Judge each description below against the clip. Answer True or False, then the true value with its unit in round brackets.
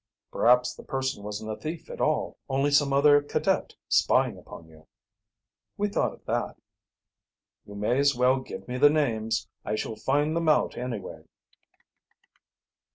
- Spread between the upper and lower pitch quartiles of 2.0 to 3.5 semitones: False (4.8 semitones)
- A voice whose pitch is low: True (130 Hz)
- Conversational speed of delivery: True (155 wpm)